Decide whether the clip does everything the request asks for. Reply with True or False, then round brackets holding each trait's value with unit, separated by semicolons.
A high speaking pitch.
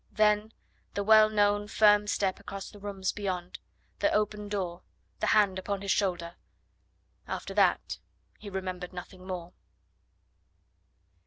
True (200 Hz)